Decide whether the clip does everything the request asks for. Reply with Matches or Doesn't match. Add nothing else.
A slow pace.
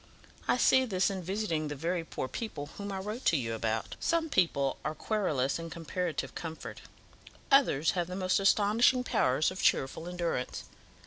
Doesn't match